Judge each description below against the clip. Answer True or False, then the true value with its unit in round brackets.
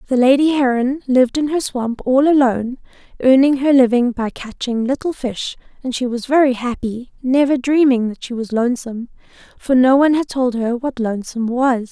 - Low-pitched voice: False (255 Hz)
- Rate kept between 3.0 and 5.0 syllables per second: False (5.4 syllables/s)